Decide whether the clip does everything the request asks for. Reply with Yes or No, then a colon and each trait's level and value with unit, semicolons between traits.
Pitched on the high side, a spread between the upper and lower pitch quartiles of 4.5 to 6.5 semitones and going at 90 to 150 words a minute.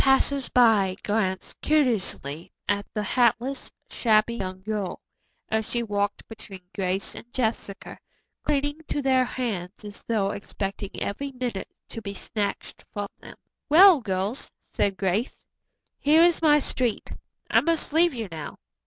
Yes: high, 220 Hz; average, 4.9 semitones; slow, 135 wpm